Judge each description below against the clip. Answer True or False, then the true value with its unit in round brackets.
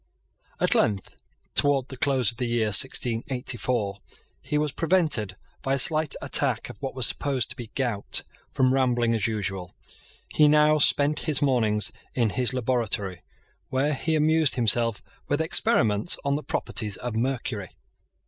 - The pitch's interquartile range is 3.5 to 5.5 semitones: True (4.3 semitones)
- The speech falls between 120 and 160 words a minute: True (150 wpm)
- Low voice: True (125 Hz)